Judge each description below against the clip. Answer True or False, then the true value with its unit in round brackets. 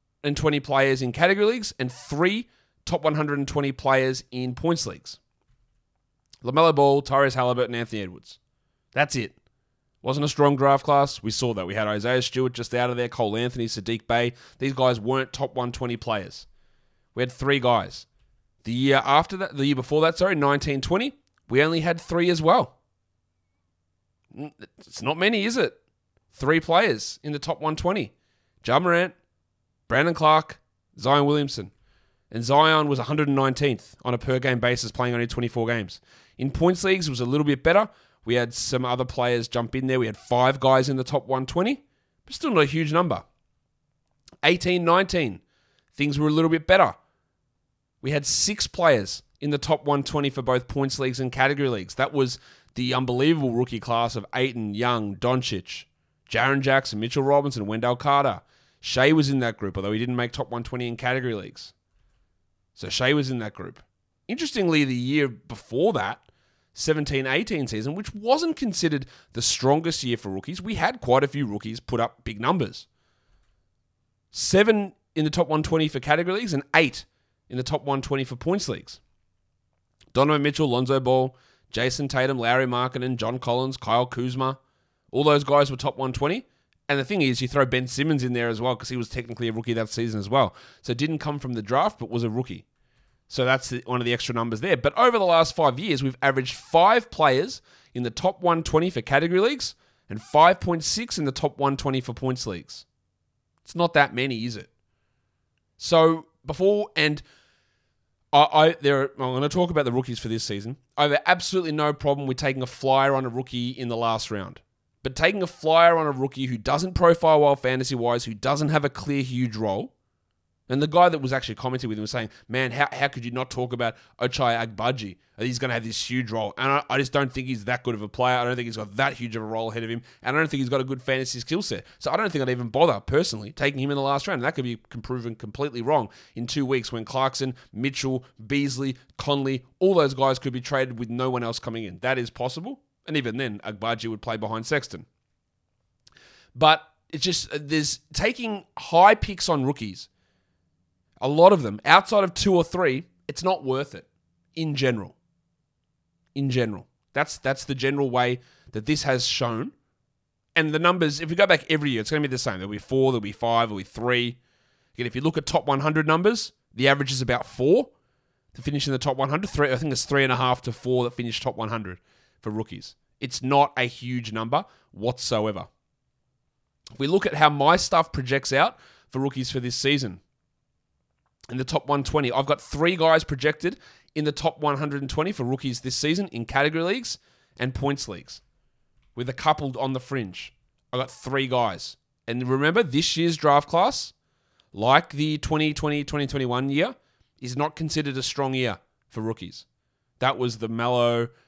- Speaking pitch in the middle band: False (130 Hz)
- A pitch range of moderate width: True (3.8 semitones)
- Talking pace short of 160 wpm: False (200 wpm)